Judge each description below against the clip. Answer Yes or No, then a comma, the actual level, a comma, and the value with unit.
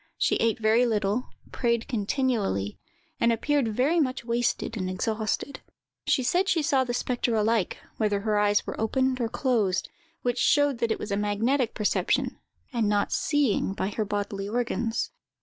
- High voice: Yes, high, 230 Hz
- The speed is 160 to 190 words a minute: Yes, average, 165 wpm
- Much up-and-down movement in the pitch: No, average, 3.5 semitones